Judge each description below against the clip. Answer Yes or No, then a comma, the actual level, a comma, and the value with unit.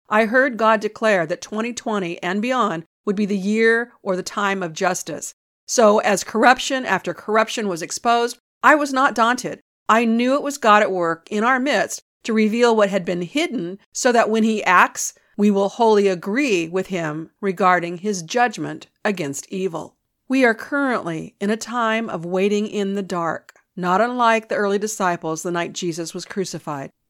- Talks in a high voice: Yes, high, 210 Hz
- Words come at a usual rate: Yes, average, 180 wpm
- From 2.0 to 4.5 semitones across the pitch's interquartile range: Yes, average, 4.0 semitones